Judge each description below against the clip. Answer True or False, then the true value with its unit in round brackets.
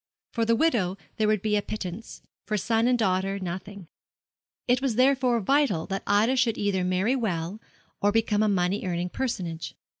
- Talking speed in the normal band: True (175 wpm)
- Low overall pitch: False (210 Hz)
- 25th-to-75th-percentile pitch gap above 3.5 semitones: True (3.9 semitones)